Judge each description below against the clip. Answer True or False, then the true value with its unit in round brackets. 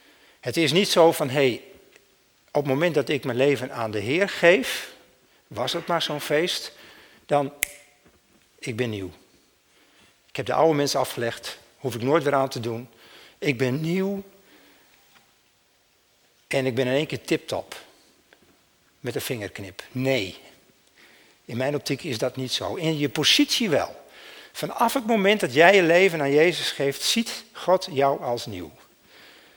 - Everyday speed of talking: True (160 wpm)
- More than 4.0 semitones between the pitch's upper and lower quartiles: True (4.5 semitones)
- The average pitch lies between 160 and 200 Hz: False (140 Hz)